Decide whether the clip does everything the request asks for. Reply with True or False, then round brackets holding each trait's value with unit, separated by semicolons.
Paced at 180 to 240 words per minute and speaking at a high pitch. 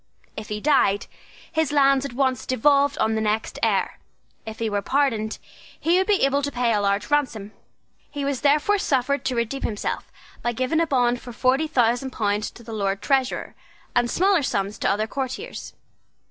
True (185 wpm; 255 Hz)